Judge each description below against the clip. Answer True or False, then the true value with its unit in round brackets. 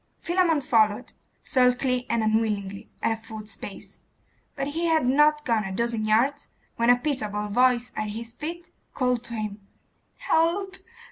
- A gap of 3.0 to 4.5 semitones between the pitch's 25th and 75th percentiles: False (5.1 semitones)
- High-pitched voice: True (245 Hz)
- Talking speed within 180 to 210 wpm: False (150 wpm)